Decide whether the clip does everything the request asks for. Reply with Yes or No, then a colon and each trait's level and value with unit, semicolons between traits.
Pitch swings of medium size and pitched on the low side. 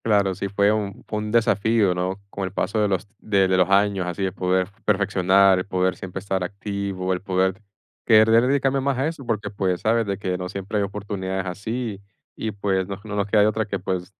No: narrow, 2.2 semitones; low, 100 Hz